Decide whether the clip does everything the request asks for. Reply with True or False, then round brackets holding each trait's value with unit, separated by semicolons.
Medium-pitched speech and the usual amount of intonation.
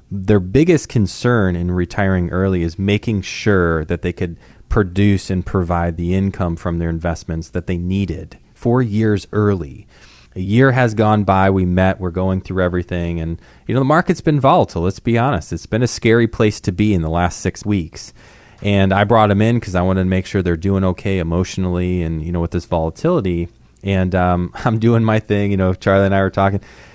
False (95 Hz; 3.2 semitones)